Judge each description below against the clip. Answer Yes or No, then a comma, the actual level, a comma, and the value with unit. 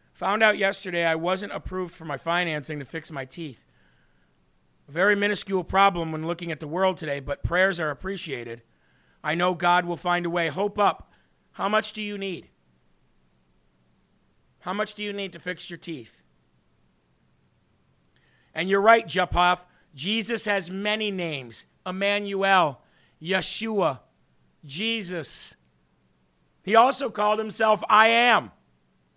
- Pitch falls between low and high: Yes, medium, 175 Hz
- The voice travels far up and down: Yes, wide, 6.0 semitones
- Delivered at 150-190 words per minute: No, average, 140 wpm